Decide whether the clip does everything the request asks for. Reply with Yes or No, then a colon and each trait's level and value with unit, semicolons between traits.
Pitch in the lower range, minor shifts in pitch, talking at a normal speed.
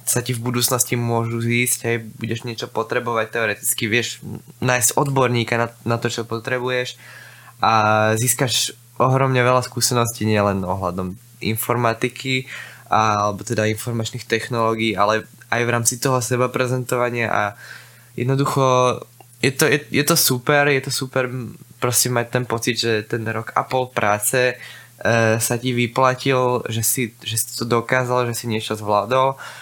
Yes: low, 120 Hz; narrow, 2.0 semitones; average, 150 wpm